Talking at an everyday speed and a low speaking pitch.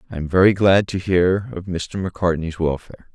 Yes: average, 190 wpm; very low, 90 Hz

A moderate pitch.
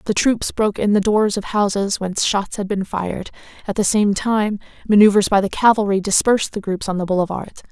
No: high, 205 Hz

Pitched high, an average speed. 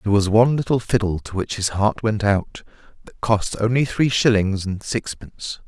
No: low, 105 Hz; average, 190 wpm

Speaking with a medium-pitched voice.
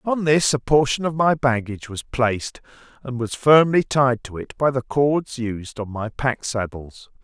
No: low, 130 Hz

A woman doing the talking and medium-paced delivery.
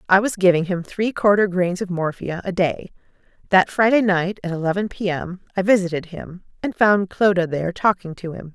Yes: female; average, 195 wpm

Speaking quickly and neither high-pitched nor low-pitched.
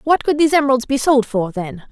No: fast, 250 wpm; very high, 255 Hz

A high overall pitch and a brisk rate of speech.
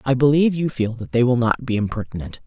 No: low, 125 Hz; fast, 245 wpm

